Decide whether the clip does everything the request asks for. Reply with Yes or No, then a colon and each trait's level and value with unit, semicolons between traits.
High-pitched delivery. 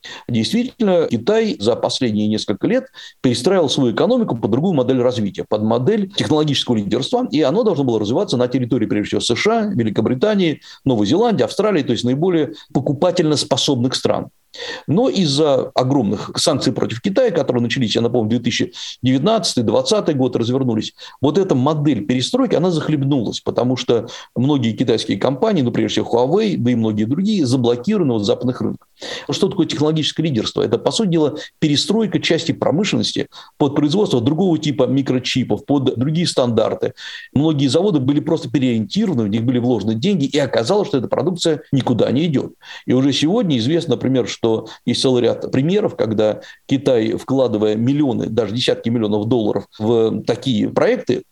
No: low, 135 Hz